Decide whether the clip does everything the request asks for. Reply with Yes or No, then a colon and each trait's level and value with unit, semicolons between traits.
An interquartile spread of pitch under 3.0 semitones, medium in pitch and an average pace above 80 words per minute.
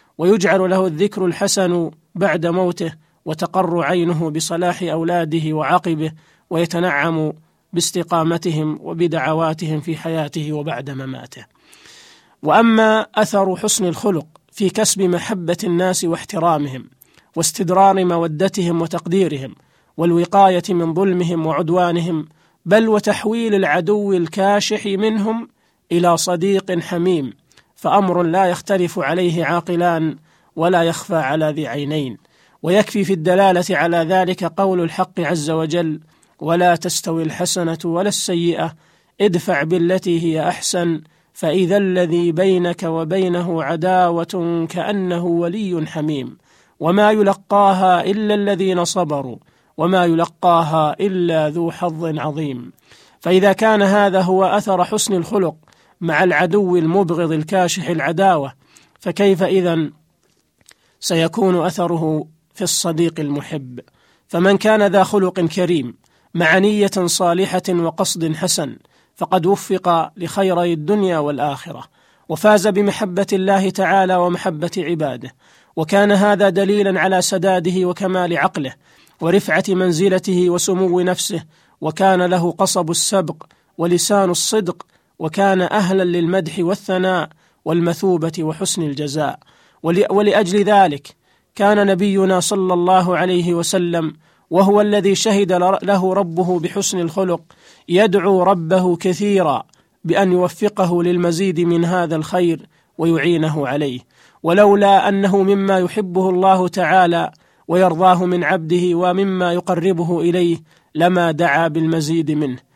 Yes: narrow, 2.4 semitones; medium, 180 Hz; average, 105 wpm